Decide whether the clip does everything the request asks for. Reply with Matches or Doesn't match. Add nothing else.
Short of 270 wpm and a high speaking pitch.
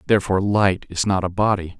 Doesn't match